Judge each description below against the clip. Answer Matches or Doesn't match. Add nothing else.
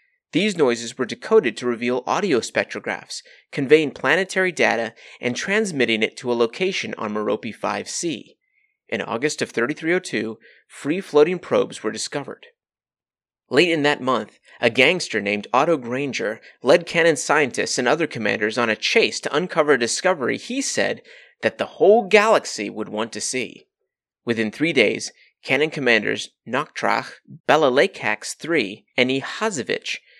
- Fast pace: Doesn't match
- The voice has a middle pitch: Matches